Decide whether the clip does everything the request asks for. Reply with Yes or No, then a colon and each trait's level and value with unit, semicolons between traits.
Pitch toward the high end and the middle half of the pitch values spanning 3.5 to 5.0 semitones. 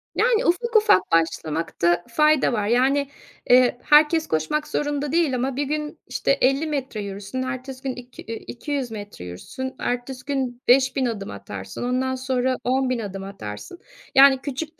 Yes: very high, 255 Hz; average, 4.3 semitones